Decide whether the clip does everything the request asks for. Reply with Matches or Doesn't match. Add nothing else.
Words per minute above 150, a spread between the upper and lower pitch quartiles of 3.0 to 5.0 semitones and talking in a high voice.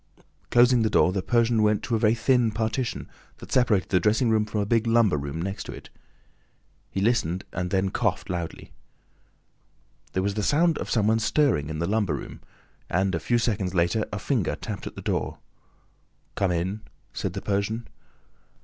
Doesn't match